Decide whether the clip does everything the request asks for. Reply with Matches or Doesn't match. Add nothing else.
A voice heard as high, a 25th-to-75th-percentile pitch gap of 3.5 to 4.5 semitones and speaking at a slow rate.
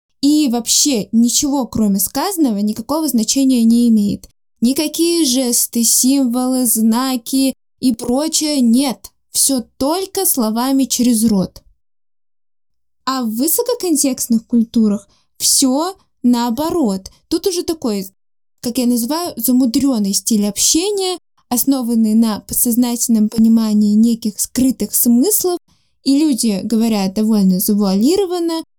Matches